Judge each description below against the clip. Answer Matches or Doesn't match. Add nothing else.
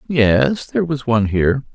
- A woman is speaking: Doesn't match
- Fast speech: Doesn't match